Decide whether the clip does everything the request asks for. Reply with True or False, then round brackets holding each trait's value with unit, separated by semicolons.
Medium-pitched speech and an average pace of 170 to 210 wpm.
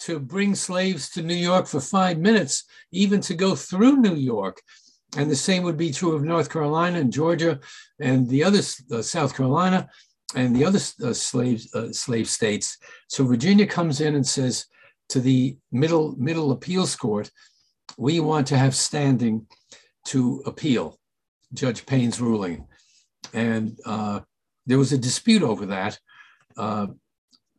False (145 Hz; 155 wpm)